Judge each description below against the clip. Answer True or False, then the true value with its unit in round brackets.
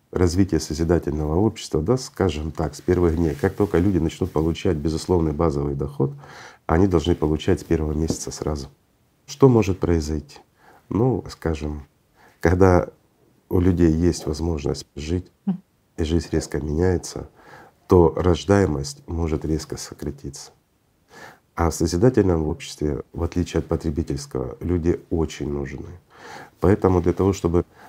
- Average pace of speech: True (125 wpm)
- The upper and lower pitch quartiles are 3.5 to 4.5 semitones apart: False (2.7 semitones)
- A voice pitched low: True (85 Hz)